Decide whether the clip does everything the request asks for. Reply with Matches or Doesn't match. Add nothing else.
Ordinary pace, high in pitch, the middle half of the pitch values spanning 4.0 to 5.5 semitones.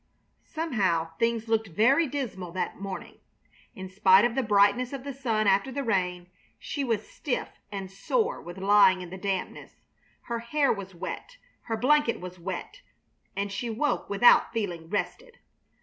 Matches